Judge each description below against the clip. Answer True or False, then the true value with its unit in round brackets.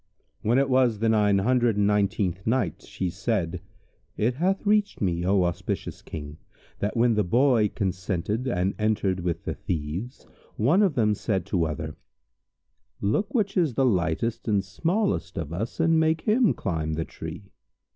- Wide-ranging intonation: True (6.0 semitones)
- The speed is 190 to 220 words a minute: False (165 wpm)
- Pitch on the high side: False (105 Hz)